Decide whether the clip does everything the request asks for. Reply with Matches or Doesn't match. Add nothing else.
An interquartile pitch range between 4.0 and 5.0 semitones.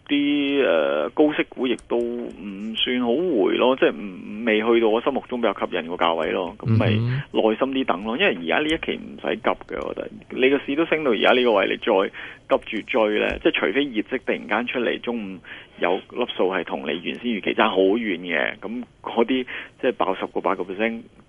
Matches